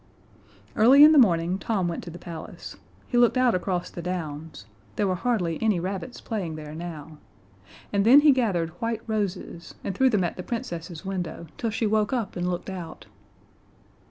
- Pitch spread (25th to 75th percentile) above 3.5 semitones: Yes, average, 4.8 semitones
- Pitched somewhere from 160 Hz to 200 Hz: Yes, medium, 185 Hz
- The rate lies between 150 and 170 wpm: No, average, 185 wpm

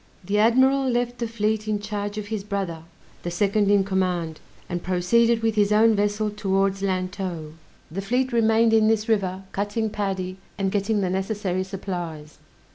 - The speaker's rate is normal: Yes, average, 165 wpm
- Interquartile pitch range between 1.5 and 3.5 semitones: Yes, narrow, 2.6 semitones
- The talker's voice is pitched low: No, high, 205 Hz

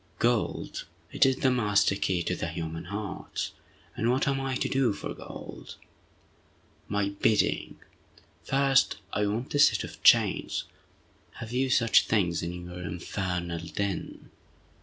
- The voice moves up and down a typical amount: No, wide, 6.1 semitones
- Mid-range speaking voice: No, low, 105 Hz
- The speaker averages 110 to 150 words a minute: Yes, average, 140 wpm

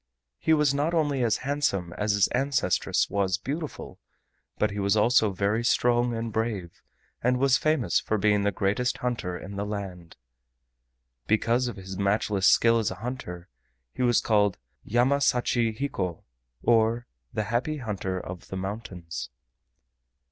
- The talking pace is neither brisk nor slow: Yes, average, 150 wpm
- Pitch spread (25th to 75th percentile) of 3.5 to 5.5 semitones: Yes, average, 4.0 semitones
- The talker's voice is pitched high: No, low, 110 Hz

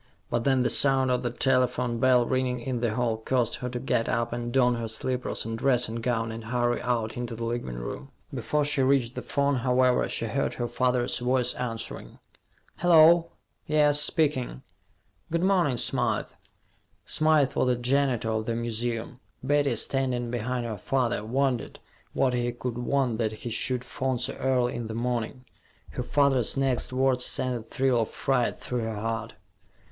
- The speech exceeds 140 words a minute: Yes, average, 175 wpm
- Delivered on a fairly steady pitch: Yes, narrow, 2.1 semitones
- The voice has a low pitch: Yes, low, 125 Hz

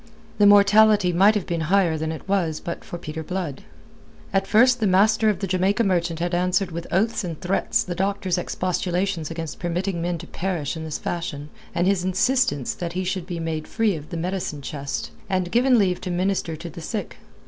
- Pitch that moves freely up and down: No, average, 2.9 semitones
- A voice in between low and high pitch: Yes, medium, 180 Hz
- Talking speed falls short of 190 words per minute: No, fast, 205 wpm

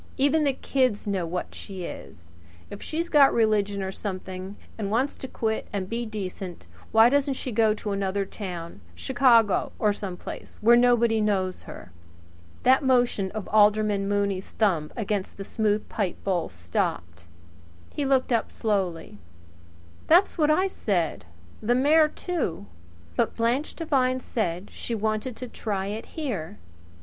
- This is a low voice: No, high, 215 Hz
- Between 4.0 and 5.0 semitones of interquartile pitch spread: Yes, average, 4.7 semitones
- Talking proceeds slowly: No, average, 150 wpm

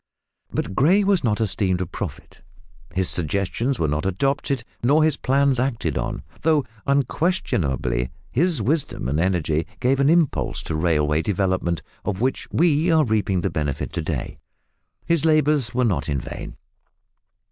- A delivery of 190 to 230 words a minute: No, average, 150 wpm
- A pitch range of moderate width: No, wide, 8.7 semitones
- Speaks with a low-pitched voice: Yes, low, 115 Hz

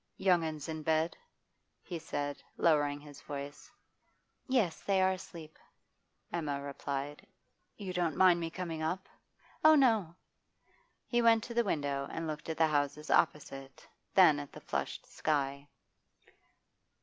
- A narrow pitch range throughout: No, average, 4.2 semitones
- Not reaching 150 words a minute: Yes, slow, 135 wpm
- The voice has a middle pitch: Yes, medium, 160 Hz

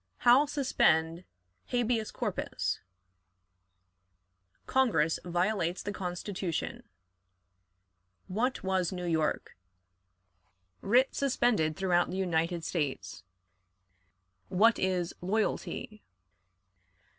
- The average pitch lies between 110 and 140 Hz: No, medium, 185 Hz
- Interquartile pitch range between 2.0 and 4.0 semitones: No, average, 4.8 semitones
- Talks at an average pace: No, slow, 75 wpm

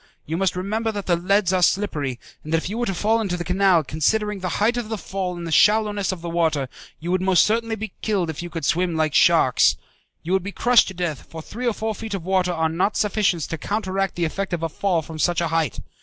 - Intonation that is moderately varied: Yes, average, 3.8 semitones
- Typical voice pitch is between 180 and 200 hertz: Yes, medium, 185 Hz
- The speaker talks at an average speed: No, fast, 260 wpm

